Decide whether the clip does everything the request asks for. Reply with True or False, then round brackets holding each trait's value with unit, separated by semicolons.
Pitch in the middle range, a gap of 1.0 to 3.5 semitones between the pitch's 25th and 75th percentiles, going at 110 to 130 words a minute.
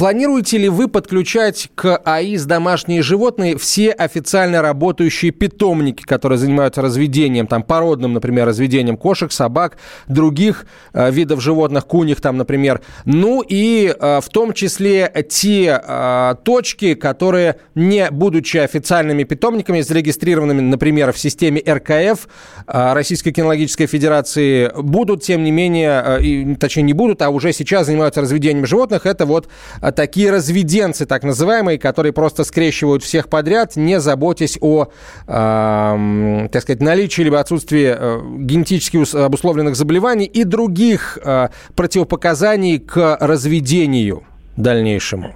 False (155 Hz; 4.5 semitones; 125 wpm)